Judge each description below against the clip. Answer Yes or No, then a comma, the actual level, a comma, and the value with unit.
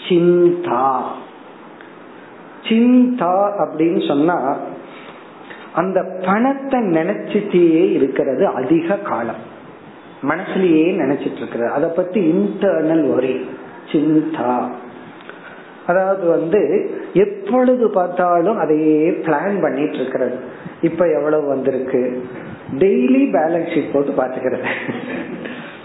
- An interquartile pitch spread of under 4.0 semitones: No, average, 5.2 semitones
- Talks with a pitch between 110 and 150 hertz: No, medium, 170 Hz